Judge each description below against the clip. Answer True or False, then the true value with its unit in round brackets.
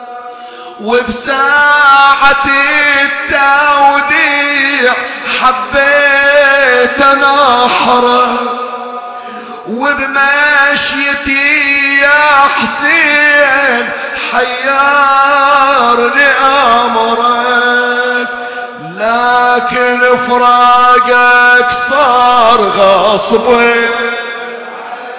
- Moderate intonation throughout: False (2.3 semitones)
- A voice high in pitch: True (245 Hz)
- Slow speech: True (30 wpm)